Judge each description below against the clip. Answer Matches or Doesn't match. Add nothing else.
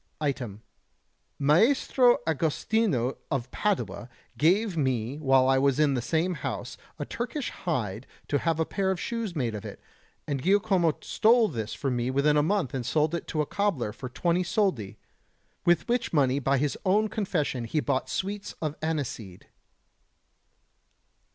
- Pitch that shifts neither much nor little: Doesn't match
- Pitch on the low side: Doesn't match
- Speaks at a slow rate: Doesn't match